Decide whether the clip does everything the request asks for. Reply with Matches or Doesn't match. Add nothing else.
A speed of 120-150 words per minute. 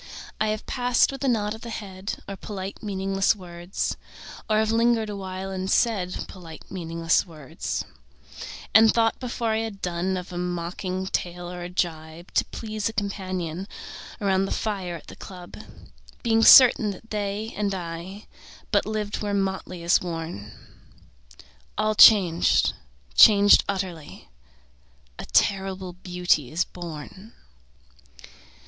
Matches